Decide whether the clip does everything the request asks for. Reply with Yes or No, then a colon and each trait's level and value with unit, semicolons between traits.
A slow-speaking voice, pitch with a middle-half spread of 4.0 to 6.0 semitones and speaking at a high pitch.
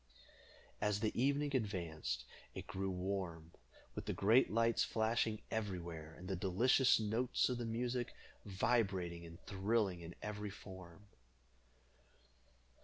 No: slow, 120 wpm; average, 4.3 semitones; low, 100 Hz